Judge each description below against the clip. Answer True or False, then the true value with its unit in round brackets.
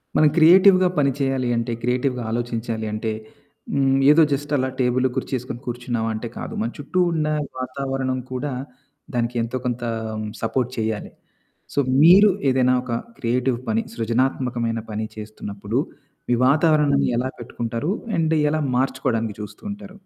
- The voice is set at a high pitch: False (125 Hz)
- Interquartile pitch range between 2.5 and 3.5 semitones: True (3.2 semitones)